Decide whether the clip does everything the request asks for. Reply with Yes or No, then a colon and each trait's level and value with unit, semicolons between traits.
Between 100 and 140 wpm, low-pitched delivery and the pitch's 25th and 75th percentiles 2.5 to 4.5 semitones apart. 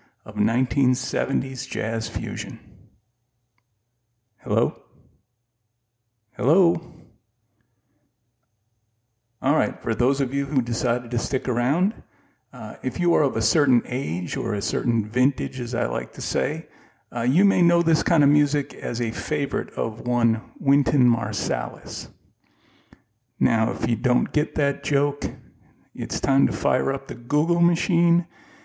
Yes: slow, 135 wpm; low, 120 Hz; average, 3.8 semitones